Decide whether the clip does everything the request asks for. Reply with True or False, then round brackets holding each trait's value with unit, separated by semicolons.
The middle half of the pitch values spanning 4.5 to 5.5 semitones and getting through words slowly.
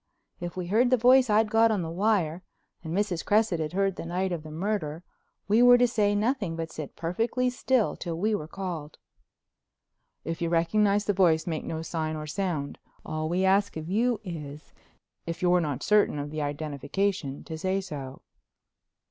False (4.8 semitones; 185 wpm)